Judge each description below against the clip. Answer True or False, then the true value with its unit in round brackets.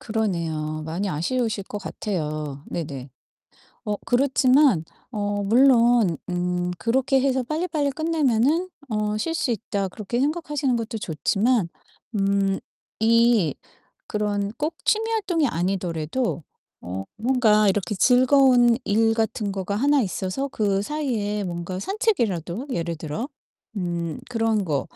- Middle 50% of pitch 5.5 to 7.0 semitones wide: True (6.0 semitones)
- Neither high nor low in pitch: False (215 Hz)